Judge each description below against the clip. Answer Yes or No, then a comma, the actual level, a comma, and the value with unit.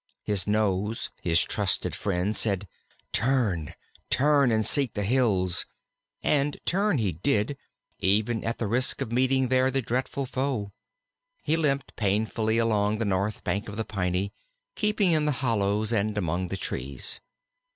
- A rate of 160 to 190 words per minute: No, average, 150 wpm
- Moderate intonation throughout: Yes, average, 4.6 semitones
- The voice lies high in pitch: No, low, 110 Hz